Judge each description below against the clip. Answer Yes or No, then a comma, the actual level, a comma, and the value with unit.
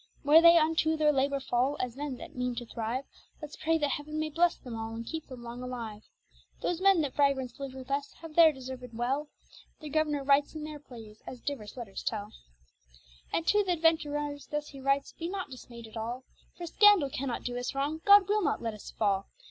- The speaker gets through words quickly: Yes, fast, 215 wpm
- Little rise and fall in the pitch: No, average, 4.1 semitones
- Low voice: No, very high, 280 Hz